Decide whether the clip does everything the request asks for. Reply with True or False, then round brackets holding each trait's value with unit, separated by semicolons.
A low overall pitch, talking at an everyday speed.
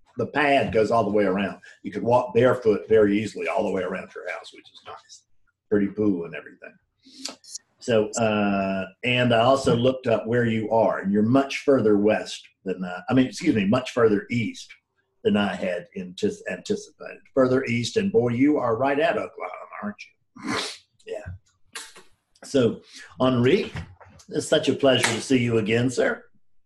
True (115 Hz; 175 wpm)